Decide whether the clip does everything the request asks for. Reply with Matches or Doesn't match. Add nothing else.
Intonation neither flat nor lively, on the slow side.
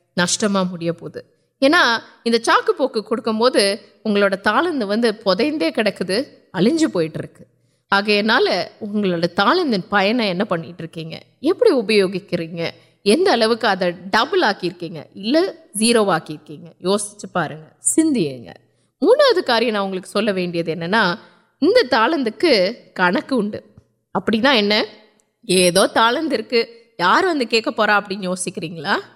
Matches